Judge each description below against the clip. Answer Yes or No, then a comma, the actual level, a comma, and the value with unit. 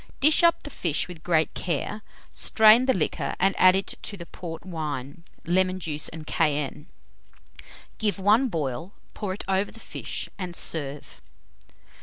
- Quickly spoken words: No, average, 155 wpm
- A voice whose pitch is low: No, medium, 180 Hz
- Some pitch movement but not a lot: Yes, average, 4.3 semitones